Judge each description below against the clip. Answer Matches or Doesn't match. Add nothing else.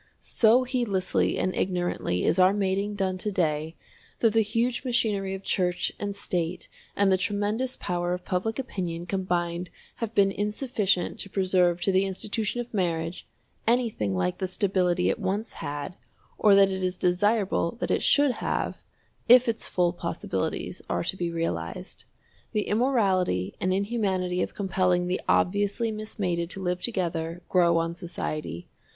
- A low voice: Doesn't match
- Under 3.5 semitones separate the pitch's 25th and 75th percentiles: Matches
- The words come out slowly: Doesn't match